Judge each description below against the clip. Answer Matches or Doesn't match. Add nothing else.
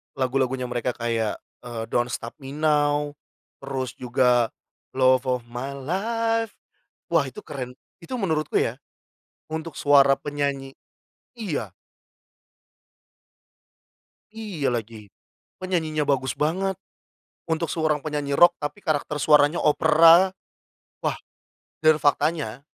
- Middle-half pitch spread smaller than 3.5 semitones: Doesn't match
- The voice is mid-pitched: Matches